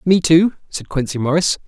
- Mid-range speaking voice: Yes, medium, 155 Hz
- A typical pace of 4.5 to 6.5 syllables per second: Yes, 5.1 syllables/s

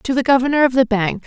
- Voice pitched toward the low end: No, high, 245 Hz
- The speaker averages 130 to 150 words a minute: No, fast, 285 wpm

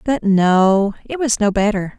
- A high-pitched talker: Yes, high, 210 Hz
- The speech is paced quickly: No, average, 180 wpm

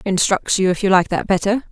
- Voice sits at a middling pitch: No, high, 195 Hz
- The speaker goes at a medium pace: No, fast, 245 wpm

